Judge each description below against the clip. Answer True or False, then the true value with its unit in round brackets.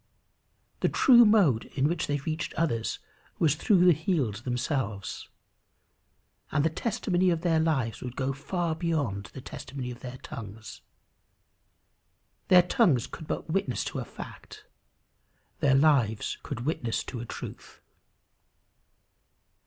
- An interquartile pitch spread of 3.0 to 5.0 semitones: False (5.4 semitones)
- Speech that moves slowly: True (130 wpm)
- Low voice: False (145 Hz)